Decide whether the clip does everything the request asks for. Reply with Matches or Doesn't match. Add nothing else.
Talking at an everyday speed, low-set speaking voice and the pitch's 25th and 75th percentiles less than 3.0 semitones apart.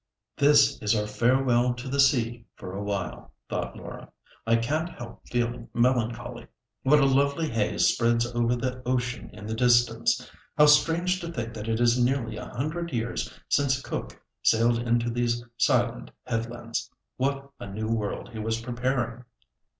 Matches